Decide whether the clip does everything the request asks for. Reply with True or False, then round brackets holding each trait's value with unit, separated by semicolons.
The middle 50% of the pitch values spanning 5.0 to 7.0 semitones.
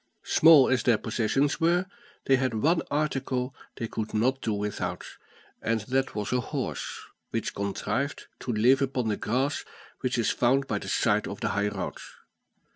False (3.7 semitones)